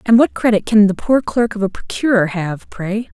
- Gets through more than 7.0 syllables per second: No, 5.0 syllables/s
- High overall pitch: Yes, high, 210 Hz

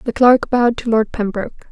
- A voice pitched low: No, high, 230 Hz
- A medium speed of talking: No, fast, 210 wpm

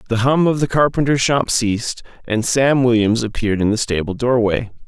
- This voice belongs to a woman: No, male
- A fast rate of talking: No, average, 185 wpm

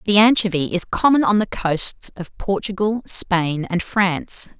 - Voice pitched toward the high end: Yes, high, 195 Hz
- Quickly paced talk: No, average, 155 wpm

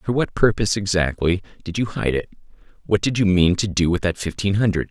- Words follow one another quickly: Yes, fast, 220 wpm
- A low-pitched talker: Yes, very low, 95 Hz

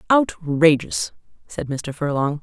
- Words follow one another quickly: No, slow, 100 wpm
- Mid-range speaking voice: Yes, medium, 160 Hz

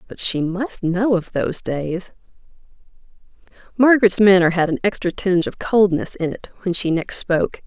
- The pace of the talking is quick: No, average, 165 wpm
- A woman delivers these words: Yes, female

